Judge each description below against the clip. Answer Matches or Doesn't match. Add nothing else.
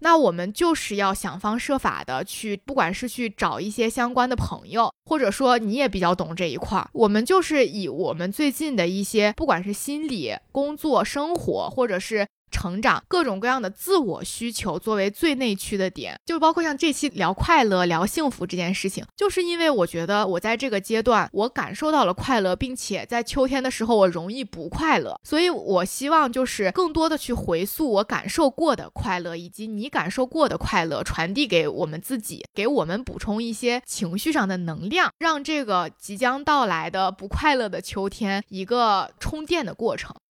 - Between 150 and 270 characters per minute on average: Doesn't match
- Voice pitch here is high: Matches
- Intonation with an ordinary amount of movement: Doesn't match